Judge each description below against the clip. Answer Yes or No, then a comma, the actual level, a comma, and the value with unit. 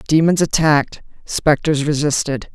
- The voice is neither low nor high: Yes, medium, 150 Hz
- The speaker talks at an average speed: No, slow, 95 wpm